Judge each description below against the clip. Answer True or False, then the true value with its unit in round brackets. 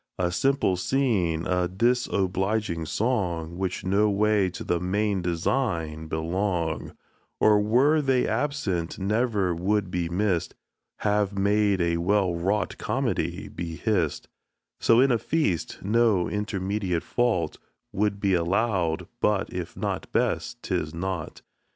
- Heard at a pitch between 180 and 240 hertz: False (95 Hz)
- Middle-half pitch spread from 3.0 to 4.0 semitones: True (3.6 semitones)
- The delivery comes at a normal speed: False (125 wpm)